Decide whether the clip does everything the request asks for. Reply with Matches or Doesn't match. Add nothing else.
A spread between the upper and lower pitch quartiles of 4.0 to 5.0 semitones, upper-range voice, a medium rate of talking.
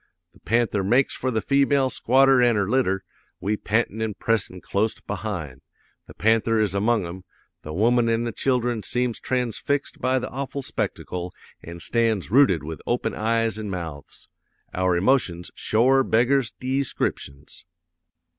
Doesn't match